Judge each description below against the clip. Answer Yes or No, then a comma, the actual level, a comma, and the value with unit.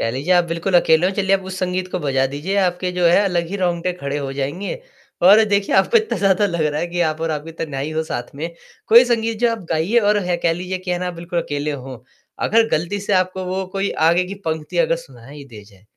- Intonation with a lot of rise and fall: No, average, 3.8 semitones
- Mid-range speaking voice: Yes, medium, 175 Hz